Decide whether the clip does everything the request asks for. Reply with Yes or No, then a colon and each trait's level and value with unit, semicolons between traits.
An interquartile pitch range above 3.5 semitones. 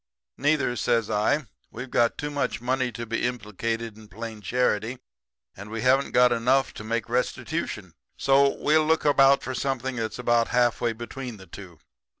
No: average, 2.9 semitones